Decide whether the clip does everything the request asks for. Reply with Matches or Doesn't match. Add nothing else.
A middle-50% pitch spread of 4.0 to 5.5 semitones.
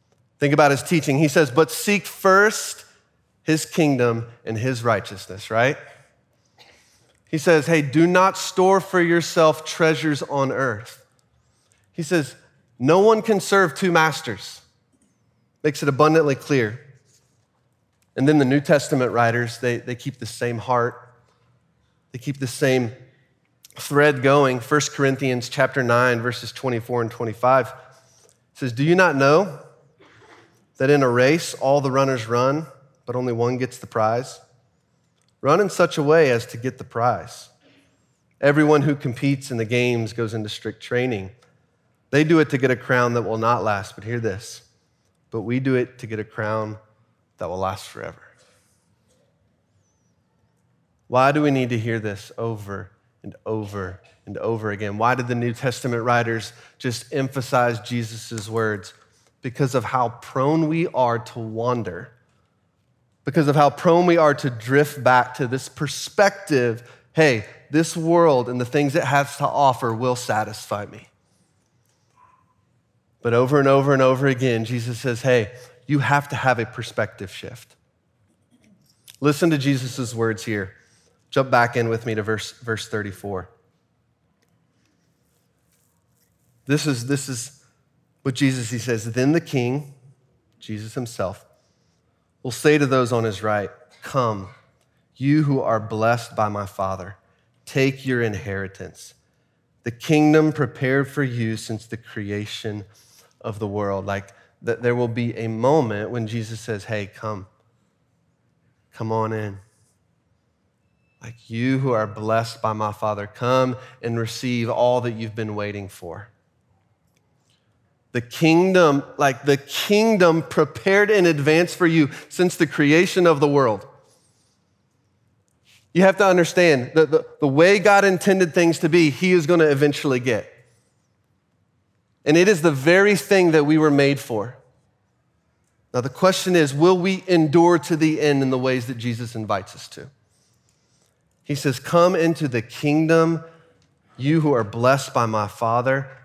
Matches